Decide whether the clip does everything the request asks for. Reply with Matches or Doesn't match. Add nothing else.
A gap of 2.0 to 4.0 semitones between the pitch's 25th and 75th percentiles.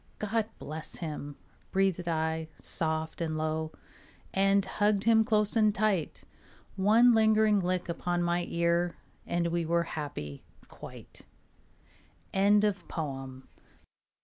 Doesn't match